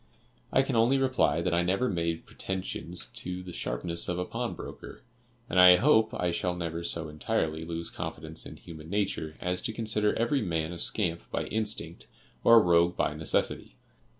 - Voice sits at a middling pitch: No, very low, 90 Hz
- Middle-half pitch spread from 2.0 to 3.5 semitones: No, average, 4.1 semitones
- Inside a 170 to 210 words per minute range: Yes, average, 180 wpm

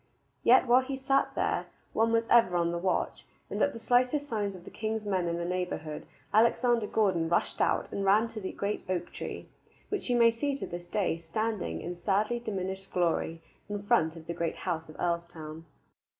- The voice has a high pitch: Yes, high, 195 Hz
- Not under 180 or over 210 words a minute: Yes, average, 195 wpm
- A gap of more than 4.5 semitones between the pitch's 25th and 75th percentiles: Yes, average, 5.1 semitones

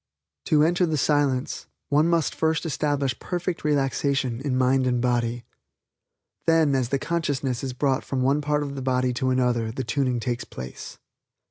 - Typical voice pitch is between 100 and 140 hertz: Yes, low, 135 Hz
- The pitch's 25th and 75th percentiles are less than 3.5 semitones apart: Yes, average, 2.8 semitones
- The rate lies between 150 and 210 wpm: Yes, average, 165 wpm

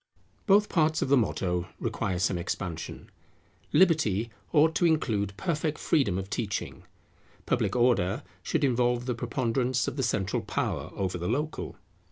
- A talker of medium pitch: No, low, 120 Hz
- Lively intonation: Yes, wide, 7.5 semitones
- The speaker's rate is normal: Yes, average, 145 wpm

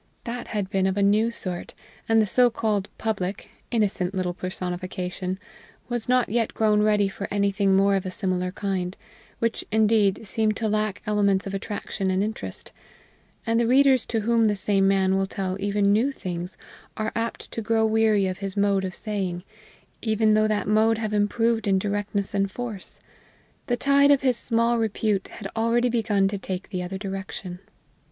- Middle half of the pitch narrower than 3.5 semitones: Yes, narrow, 2.5 semitones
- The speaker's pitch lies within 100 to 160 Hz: No, high, 205 Hz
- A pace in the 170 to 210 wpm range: Yes, average, 180 wpm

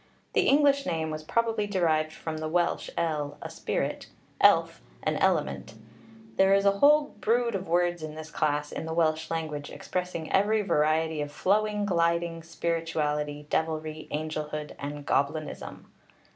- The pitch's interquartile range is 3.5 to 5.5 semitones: Yes, average, 3.8 semitones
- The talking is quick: No, average, 145 wpm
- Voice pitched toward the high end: No, medium, 160 Hz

